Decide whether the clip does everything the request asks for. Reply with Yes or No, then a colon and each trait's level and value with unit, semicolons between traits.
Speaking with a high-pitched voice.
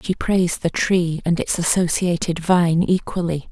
No: medium, 175 Hz